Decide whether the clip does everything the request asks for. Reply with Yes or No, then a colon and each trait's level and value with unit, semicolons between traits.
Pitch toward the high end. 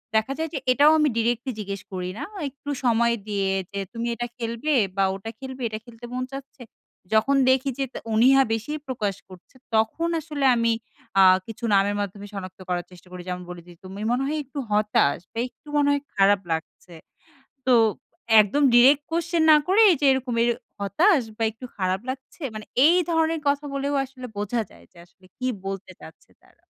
Yes: high, 235 Hz